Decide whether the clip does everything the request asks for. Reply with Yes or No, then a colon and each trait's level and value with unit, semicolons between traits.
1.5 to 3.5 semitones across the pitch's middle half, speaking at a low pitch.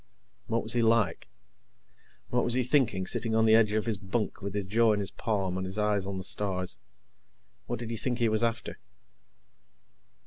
Yes: average, 2.9 semitones; low, 110 Hz